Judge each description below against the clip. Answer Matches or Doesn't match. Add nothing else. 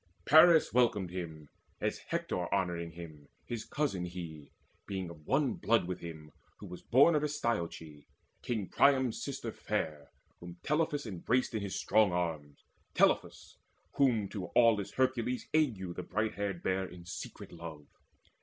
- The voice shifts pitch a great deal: Matches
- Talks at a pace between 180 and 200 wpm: Doesn't match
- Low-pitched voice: Matches